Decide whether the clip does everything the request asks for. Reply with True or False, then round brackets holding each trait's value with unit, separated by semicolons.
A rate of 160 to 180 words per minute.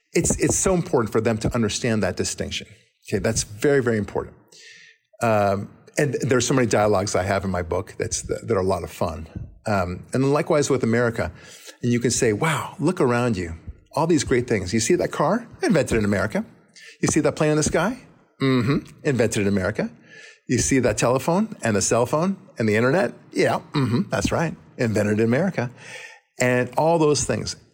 False (195 wpm)